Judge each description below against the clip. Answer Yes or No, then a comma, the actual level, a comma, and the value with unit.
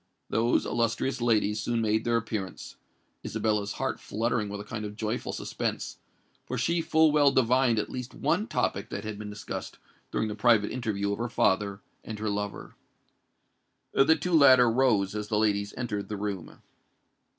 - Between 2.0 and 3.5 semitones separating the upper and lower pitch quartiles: Yes, average, 2.8 semitones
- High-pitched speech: No, low, 110 Hz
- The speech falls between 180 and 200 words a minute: No, average, 165 wpm